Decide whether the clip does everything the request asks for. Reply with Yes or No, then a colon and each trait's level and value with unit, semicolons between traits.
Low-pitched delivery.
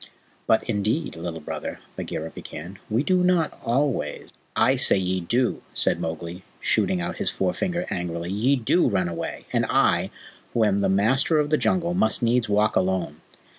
Yes: low, 110 Hz